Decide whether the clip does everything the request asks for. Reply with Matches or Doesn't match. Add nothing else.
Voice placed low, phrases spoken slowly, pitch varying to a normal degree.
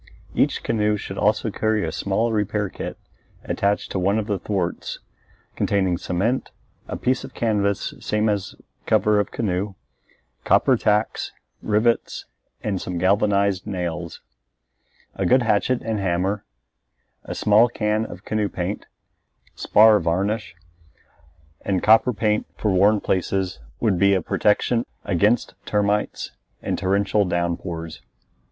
Doesn't match